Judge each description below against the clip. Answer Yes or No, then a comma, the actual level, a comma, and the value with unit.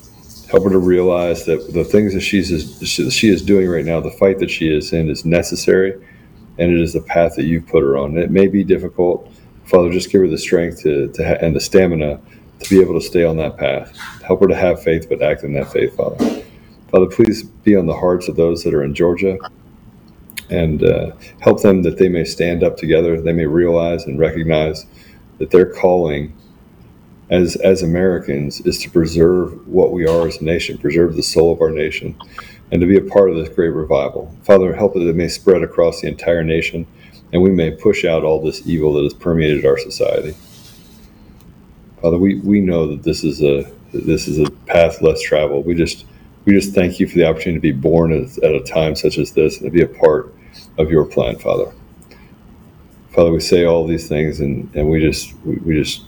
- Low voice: Yes, very low, 85 Hz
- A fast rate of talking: Yes, fast, 220 wpm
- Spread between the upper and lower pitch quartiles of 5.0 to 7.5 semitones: No, average, 2.9 semitones